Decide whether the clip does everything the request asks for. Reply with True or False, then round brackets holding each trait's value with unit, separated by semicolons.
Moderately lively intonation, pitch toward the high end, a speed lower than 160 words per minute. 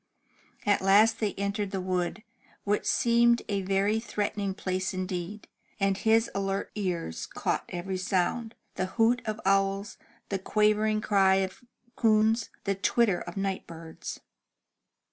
False (2.2 semitones; 200 Hz; 140 wpm)